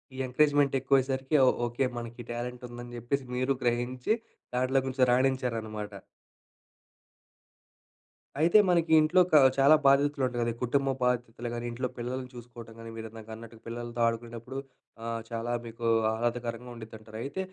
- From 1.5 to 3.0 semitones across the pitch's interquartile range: Yes, narrow, 2.4 semitones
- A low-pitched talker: Yes, low, 120 Hz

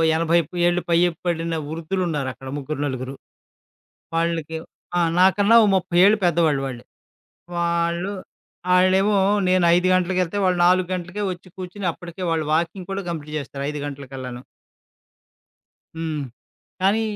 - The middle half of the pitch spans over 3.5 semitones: No, average, 3.2 semitones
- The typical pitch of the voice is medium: Yes, medium, 170 Hz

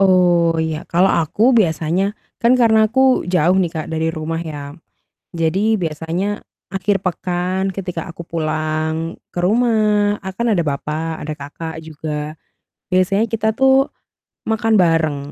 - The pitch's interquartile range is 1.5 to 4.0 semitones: No, average, 4.4 semitones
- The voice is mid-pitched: Yes, medium, 175 Hz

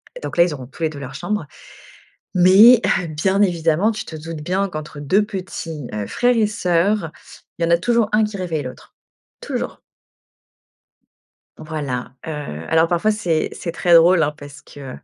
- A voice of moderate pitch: Yes, medium, 170 Hz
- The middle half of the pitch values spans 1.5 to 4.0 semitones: No, average, 4.7 semitones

